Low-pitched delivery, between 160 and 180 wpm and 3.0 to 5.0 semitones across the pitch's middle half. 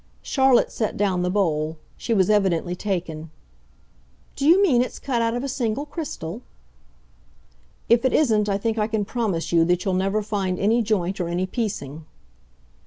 No: high, 205 Hz; average, 175 wpm; average, 4.6 semitones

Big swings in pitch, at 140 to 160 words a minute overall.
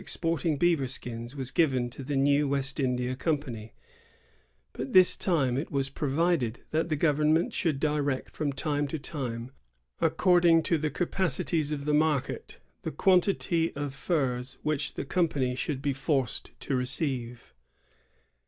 No: average, 3.5 semitones; average, 155 wpm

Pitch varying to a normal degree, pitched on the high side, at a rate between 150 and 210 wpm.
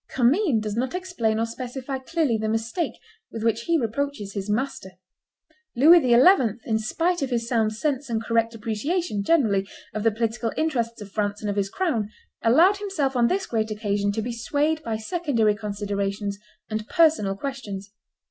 Yes: average, 4.9 semitones; high, 230 Hz; average, 170 wpm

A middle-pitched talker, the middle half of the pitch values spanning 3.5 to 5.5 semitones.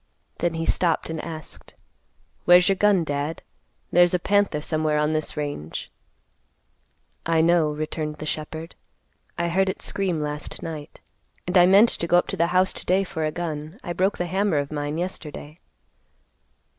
No: medium, 165 Hz; average, 2.8 semitones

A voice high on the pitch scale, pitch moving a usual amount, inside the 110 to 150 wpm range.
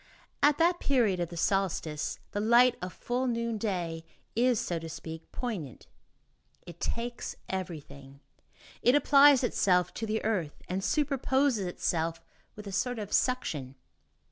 No: high, 205 Hz; wide, 6.5 semitones; average, 140 wpm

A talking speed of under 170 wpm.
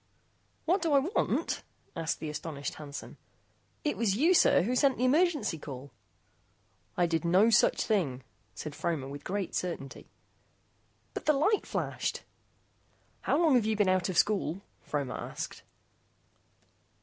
Yes: average, 150 wpm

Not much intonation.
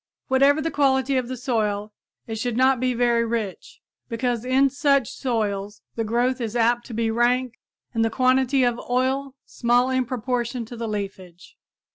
Yes: narrow, 2.3 semitones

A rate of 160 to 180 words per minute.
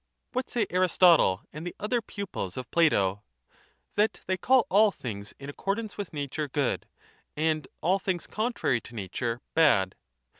No: average, 150 wpm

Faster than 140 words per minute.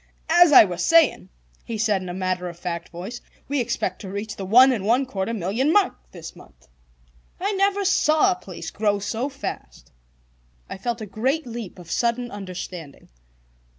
Yes: average, 180 wpm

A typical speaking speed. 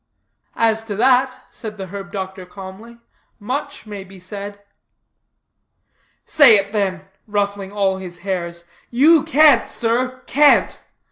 No: slow, 125 wpm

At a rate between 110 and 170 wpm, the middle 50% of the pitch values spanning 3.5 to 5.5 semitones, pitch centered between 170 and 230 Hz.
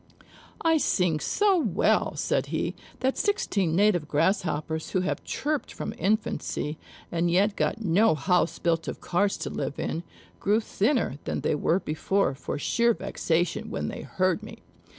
Yes: average, 155 wpm; average, 4.7 semitones; medium, 185 Hz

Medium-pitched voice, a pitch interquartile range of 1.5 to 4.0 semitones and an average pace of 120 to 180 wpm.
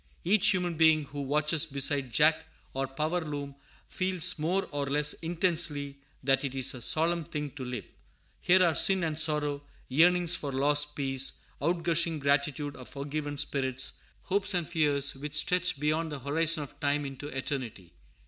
Yes: medium, 150 Hz; average, 2.9 semitones; average, 160 wpm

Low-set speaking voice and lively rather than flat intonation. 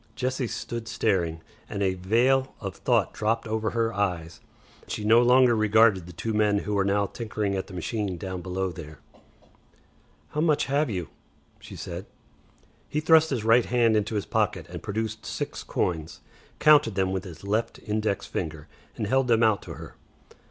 No: low, 105 Hz; average, 3.7 semitones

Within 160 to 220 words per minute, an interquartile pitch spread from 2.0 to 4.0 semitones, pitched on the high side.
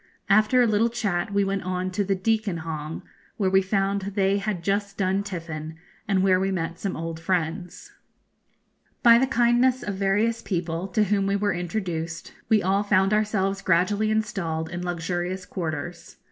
Yes: average, 170 wpm; average, 2.9 semitones; high, 195 Hz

